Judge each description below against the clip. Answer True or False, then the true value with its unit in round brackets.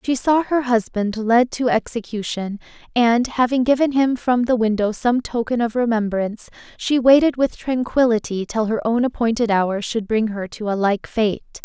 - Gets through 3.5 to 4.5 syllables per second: False (4.7 syllables/s)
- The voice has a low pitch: False (230 Hz)